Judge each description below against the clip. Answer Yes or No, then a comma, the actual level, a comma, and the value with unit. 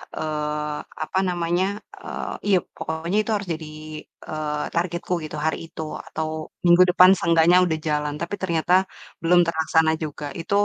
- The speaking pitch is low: No, medium, 165 Hz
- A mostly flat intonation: Yes, narrow, 2.2 semitones